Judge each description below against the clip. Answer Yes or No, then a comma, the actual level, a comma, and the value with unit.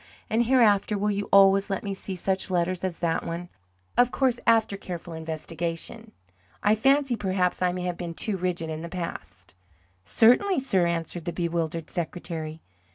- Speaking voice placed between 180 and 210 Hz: Yes, medium, 185 Hz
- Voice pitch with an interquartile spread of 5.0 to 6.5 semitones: No, average, 3.7 semitones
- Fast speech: No, average, 165 wpm